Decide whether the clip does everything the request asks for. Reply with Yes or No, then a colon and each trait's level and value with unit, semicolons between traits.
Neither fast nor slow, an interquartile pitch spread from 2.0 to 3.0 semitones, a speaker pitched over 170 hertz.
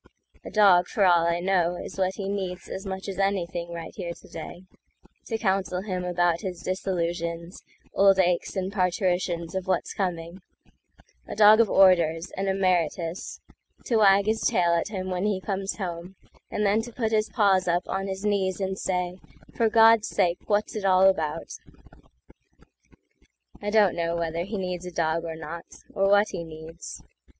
Yes: average, 155 wpm; narrow, 2.4 semitones; medium, 185 Hz